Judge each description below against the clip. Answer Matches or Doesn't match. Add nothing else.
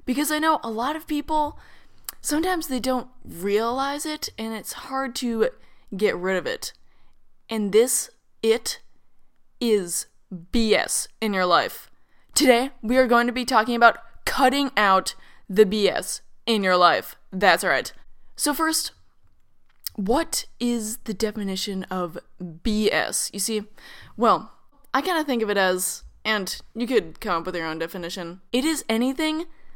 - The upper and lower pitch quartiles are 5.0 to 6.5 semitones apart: Matches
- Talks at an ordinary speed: Matches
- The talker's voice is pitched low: Doesn't match